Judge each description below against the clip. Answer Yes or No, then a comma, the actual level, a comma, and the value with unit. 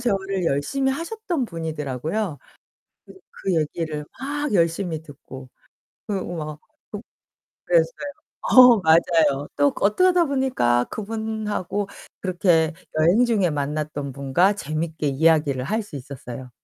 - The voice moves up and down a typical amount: No, wide, 6.7 semitones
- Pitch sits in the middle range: Yes, medium, 170 Hz